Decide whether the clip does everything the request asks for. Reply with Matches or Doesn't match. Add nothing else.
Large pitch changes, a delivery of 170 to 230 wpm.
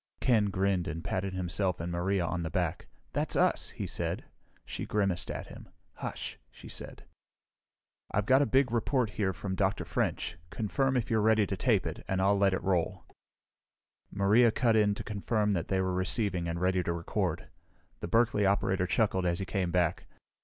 Doesn't match